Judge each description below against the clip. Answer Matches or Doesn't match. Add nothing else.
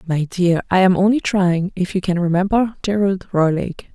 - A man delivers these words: Doesn't match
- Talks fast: Doesn't match